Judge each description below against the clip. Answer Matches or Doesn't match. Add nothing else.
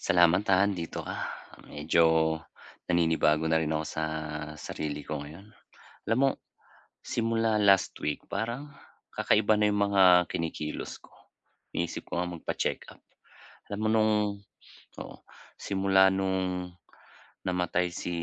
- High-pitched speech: Doesn't match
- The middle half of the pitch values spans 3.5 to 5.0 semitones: Matches